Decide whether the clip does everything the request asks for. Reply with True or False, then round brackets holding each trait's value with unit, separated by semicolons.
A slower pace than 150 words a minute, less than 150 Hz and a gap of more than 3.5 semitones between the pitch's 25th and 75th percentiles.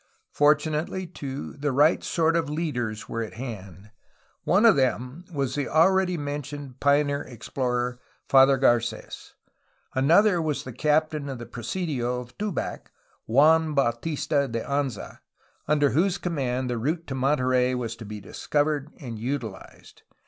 True (140 wpm; 140 Hz; 3.9 semitones)